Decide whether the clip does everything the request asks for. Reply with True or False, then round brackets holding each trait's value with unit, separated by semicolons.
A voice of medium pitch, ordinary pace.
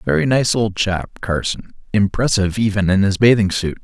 False (100 Hz; 170 wpm)